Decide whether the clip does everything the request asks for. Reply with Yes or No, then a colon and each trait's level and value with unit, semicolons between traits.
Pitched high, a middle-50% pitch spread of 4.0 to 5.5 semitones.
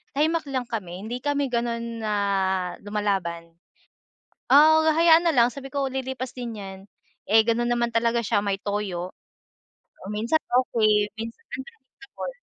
Yes: high, 235 Hz; average, 4.5 semitones